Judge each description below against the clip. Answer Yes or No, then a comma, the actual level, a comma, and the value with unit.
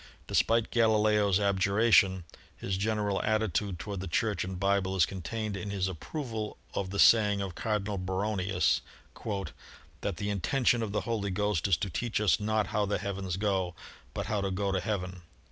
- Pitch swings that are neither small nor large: No, narrow, 2.2 semitones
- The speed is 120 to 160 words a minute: No, average, 175 wpm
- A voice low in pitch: Yes, low, 100 Hz